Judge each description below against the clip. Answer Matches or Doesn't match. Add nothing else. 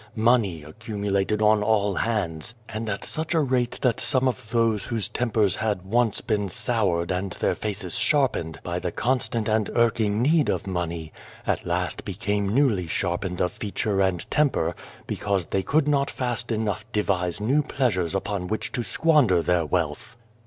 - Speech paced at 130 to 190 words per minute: Matches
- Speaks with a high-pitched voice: Doesn't match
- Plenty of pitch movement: Doesn't match